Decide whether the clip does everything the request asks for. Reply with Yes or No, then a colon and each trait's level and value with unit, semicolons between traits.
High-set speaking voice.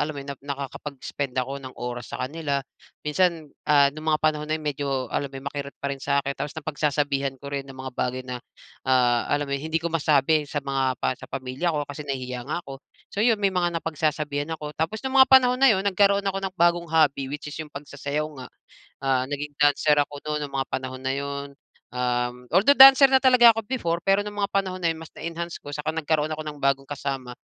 No: medium, 145 Hz